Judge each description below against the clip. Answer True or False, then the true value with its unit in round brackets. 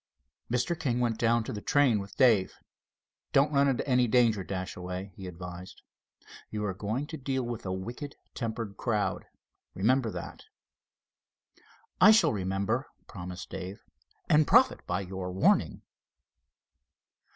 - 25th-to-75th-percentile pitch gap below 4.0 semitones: False (5.4 semitones)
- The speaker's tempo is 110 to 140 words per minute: True (135 wpm)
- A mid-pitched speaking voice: False (110 Hz)